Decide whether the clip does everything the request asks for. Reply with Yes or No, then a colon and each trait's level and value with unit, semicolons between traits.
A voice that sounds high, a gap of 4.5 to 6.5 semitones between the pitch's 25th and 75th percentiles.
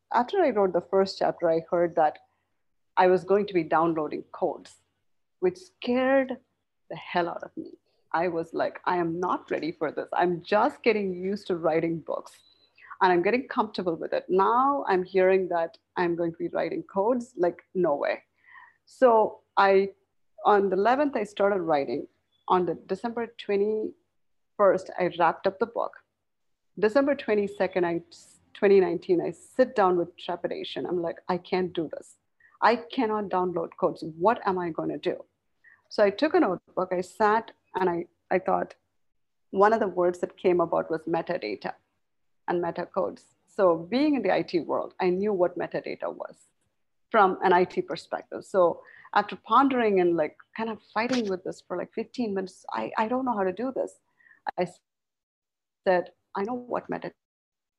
Yes: high, 195 Hz; average, 4.9 semitones